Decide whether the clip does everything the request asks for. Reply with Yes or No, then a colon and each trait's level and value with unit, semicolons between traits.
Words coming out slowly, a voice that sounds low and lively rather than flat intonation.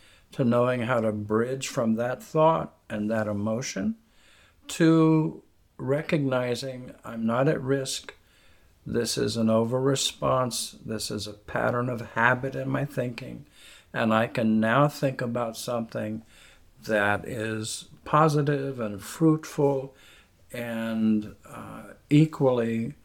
No: slow, 120 wpm; low, 120 Hz; average, 3.8 semitones